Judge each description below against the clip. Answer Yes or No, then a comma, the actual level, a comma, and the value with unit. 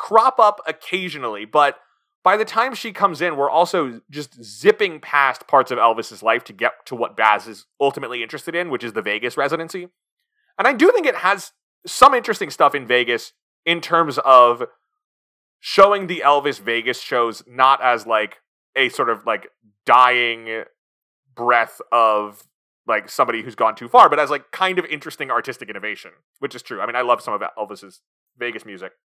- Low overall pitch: No, medium, 160 Hz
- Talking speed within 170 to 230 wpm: Yes, average, 180 wpm